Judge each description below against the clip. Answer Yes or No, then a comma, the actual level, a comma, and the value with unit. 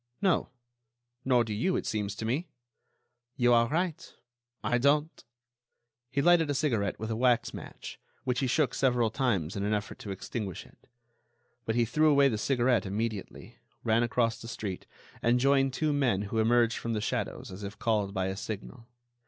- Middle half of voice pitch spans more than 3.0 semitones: Yes, average, 4.0 semitones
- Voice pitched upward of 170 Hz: No, low, 120 Hz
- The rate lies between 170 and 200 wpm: Yes, average, 180 wpm